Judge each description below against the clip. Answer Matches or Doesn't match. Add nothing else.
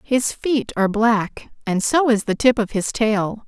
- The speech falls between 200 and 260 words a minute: Matches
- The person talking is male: Doesn't match